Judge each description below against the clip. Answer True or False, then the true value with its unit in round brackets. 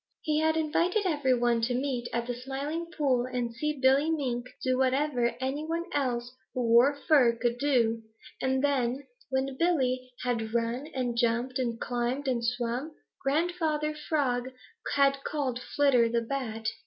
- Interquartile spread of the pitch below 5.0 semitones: True (3.2 semitones)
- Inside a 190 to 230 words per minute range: False (155 wpm)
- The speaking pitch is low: False (260 Hz)